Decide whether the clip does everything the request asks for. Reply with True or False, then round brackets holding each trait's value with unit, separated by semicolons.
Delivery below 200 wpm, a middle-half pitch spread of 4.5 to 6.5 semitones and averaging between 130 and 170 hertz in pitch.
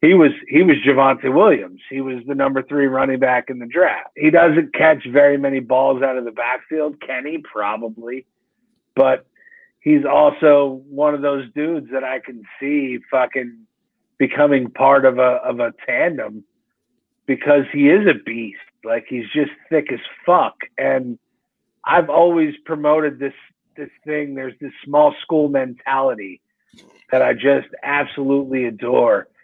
False (155 wpm; 2.5 semitones; 140 Hz)